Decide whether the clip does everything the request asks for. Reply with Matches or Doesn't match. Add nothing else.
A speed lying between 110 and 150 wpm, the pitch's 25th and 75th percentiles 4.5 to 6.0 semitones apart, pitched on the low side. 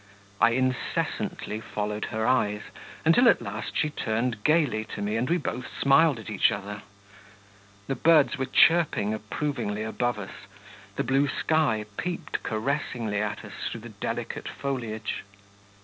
Matches